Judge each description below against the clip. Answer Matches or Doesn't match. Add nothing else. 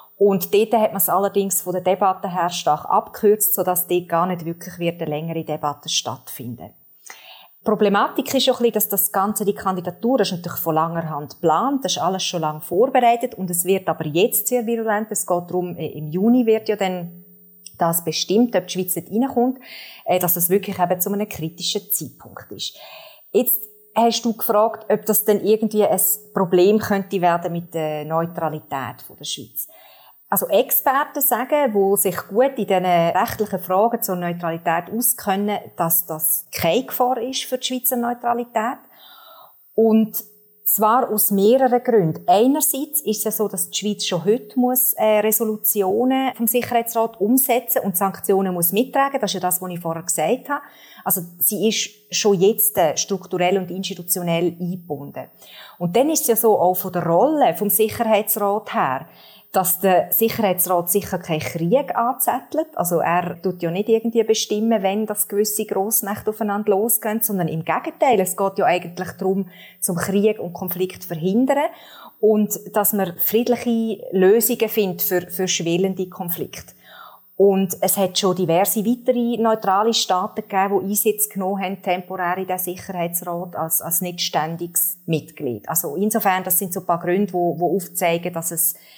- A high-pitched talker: Matches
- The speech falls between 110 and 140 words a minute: Doesn't match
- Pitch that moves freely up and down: Doesn't match